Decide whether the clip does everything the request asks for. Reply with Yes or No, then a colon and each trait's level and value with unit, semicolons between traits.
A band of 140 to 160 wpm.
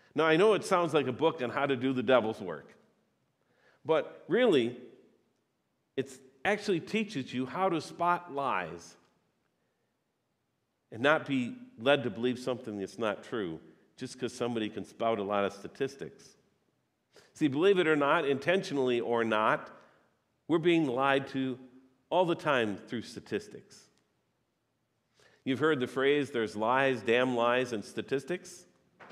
Yes: average, 145 wpm